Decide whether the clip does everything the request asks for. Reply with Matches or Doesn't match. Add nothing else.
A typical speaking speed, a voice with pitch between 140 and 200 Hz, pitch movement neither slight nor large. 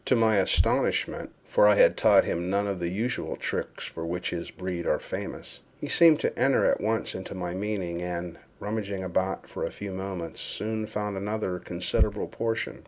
Doesn't match